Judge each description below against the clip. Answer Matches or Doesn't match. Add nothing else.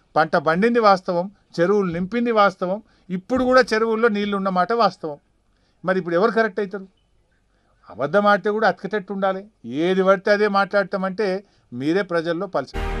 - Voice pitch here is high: Matches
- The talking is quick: Matches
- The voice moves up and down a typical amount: Matches